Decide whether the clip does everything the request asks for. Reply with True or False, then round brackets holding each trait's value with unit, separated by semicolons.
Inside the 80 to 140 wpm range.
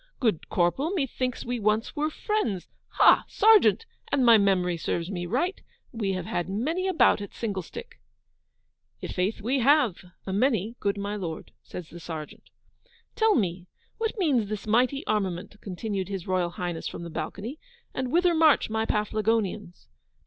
False (160 wpm)